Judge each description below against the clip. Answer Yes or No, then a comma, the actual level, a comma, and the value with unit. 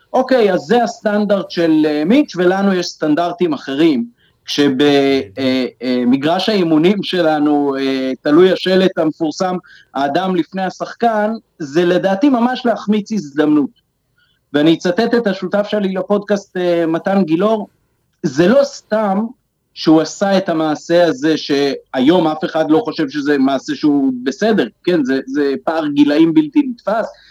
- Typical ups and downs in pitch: No, wide, 5.7 semitones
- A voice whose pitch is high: No, medium, 175 Hz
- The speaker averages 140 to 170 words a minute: No, average, 125 wpm